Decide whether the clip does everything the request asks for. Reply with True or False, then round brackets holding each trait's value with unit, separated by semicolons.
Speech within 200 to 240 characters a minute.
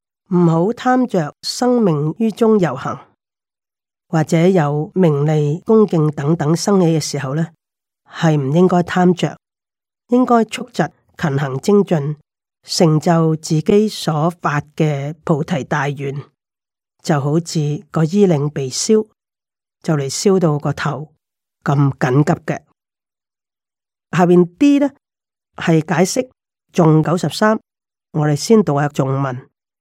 False (175 characters per minute)